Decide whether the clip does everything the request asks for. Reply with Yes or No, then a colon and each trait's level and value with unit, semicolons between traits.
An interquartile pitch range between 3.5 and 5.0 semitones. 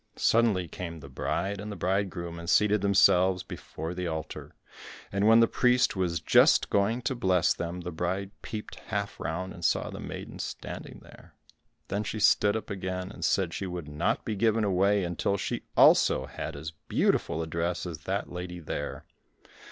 No: average, 3.1 semitones